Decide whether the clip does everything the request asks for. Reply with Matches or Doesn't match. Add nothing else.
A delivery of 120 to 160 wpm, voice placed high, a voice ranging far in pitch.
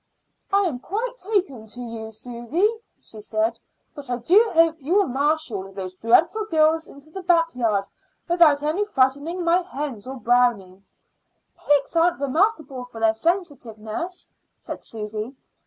Matches